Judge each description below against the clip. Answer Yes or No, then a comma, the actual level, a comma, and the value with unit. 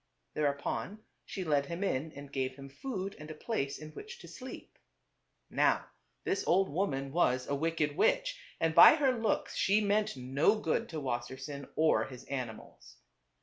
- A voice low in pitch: No, medium, 155 Hz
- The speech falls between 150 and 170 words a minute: Yes, average, 165 wpm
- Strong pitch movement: Yes, wide, 6.5 semitones